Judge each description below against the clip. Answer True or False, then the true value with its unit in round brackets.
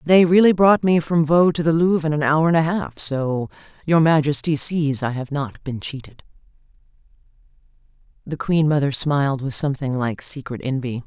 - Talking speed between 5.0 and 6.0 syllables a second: True (5.1 syllables/s)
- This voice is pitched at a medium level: True (150 Hz)